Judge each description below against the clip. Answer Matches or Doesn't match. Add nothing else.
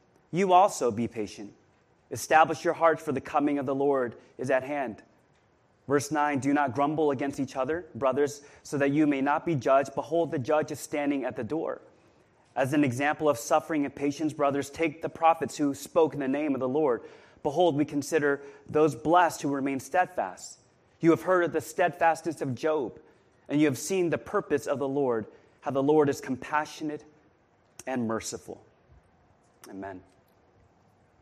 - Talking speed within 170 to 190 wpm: Matches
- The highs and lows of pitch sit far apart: Doesn't match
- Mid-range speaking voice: Matches